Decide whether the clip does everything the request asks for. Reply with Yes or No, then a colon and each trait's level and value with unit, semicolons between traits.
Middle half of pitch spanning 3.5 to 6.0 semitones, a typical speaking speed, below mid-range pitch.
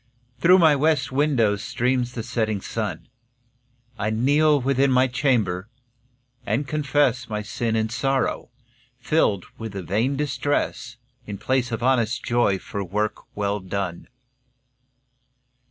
No: average, 4.2 semitones; slow, 120 wpm; low, 120 Hz